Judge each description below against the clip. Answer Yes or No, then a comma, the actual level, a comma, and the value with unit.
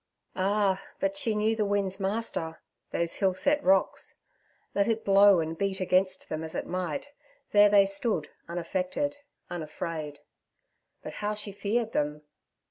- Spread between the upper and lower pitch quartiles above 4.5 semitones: No, average, 3.4 semitones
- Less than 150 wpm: Yes, average, 140 wpm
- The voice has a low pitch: No, high, 195 Hz